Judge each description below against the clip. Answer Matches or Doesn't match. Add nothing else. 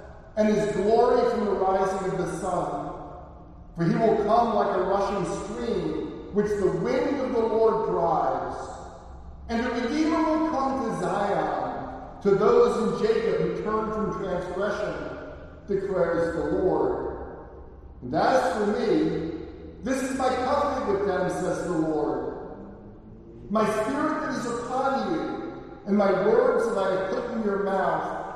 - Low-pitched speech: Doesn't match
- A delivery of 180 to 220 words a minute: Doesn't match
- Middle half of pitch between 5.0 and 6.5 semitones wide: Matches